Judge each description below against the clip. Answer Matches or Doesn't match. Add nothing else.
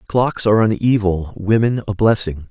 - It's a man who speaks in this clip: Matches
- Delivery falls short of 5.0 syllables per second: Matches